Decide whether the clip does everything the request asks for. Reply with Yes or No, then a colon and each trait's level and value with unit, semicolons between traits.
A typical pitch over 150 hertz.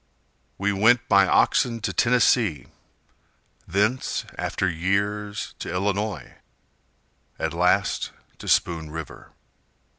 No: low, 100 Hz